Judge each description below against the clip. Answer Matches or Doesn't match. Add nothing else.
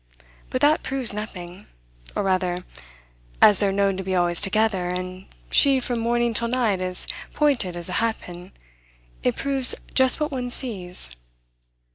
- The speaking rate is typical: Matches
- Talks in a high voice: Matches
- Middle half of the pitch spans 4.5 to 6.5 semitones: Matches